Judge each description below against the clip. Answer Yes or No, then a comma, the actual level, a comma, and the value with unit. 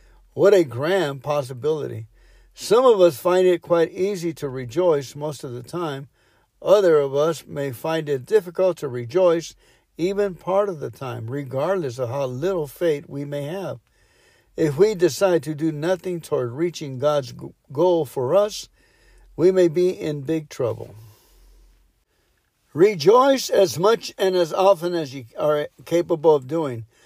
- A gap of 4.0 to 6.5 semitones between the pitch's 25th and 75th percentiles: Yes, average, 4.5 semitones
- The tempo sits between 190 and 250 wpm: No, average, 155 wpm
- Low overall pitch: No, medium, 160 Hz